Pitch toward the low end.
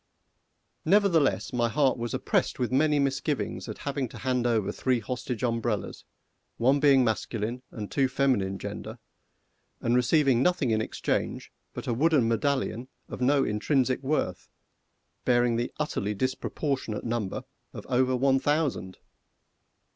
Yes: low, 130 Hz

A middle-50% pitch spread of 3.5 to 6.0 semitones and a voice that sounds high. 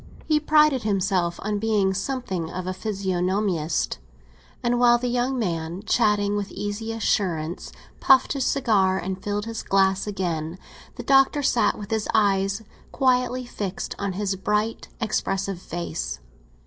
Yes: average, 3.8 semitones; high, 205 Hz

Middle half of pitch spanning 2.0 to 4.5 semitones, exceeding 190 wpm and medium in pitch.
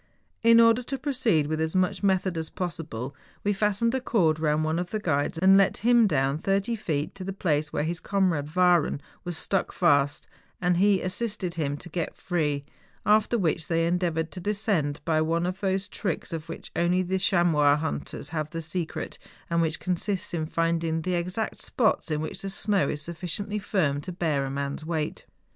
Yes: average, 3.8 semitones; fast, 205 wpm; medium, 175 Hz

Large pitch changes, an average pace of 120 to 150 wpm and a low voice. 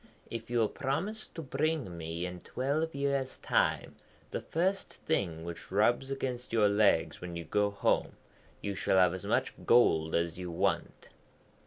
No: wide, 7.5 semitones; average, 165 wpm; low, 110 Hz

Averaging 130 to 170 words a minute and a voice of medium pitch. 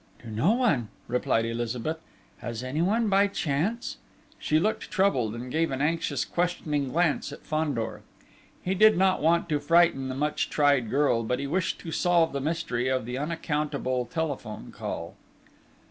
Yes: average, 160 wpm; medium, 150 Hz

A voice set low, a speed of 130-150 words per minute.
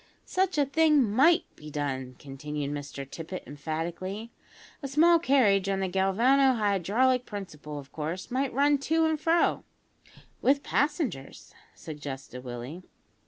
No: high, 195 Hz; slow, 135 wpm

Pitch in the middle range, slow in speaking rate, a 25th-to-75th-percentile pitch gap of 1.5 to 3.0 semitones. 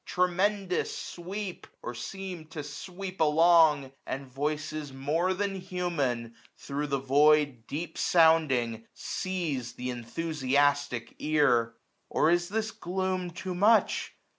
No: medium, 155 Hz; slow, 115 wpm; average, 4.8 semitones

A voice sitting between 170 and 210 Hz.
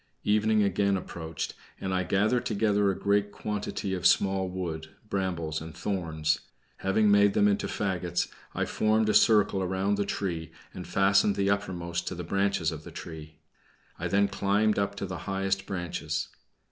No: very low, 95 Hz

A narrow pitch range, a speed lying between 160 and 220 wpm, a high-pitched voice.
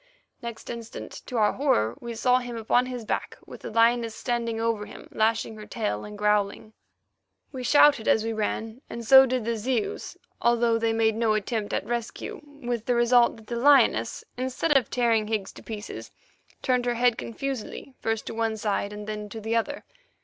Yes: narrow, 2.0 semitones; average, 190 wpm; high, 230 Hz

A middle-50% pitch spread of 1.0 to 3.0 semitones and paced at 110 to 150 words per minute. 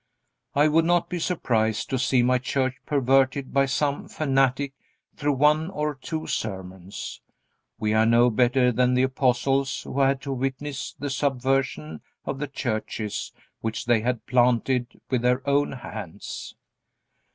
Yes: narrow, 2.6 semitones; average, 145 wpm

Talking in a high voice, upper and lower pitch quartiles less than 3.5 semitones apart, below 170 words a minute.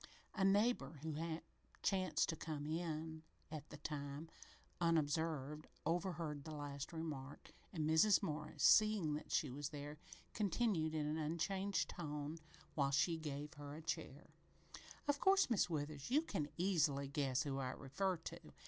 No: medium, 155 Hz; average, 2.9 semitones; average, 150 wpm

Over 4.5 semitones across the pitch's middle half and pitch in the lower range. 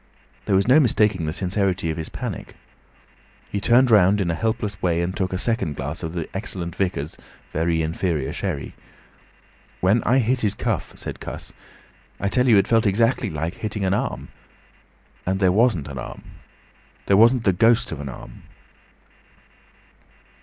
Yes: average, 4.9 semitones; very low, 95 Hz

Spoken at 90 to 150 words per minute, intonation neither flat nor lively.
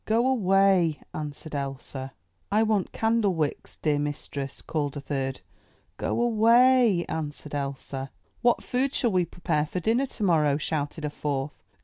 No: slow, 135 wpm; wide, 7.2 semitones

